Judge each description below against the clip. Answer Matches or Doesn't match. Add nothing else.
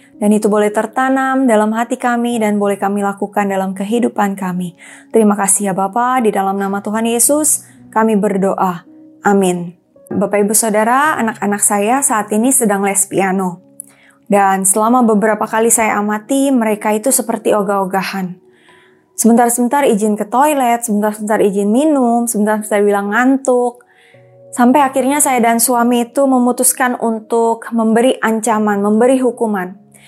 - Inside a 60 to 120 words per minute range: Doesn't match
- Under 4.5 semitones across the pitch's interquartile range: Matches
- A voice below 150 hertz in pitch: Doesn't match